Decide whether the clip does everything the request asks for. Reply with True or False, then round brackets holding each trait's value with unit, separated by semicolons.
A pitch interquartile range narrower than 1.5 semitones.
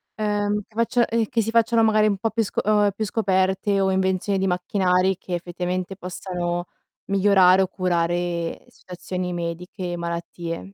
False (2.6 semitones)